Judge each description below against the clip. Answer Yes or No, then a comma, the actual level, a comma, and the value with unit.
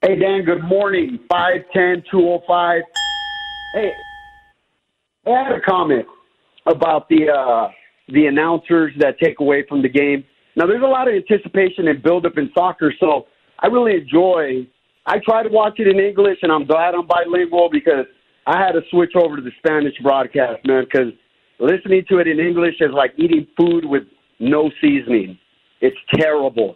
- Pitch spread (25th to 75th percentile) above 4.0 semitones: Yes, average, 4.5 semitones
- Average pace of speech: Yes, average, 175 wpm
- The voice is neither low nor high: Yes, medium, 170 Hz